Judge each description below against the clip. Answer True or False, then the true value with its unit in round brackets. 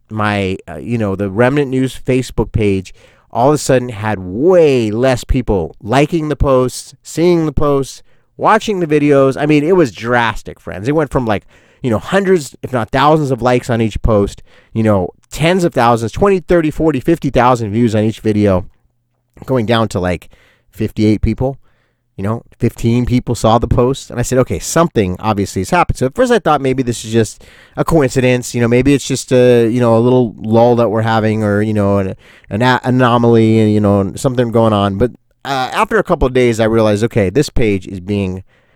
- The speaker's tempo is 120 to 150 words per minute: False (205 wpm)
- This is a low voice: True (120 Hz)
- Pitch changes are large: False (3.7 semitones)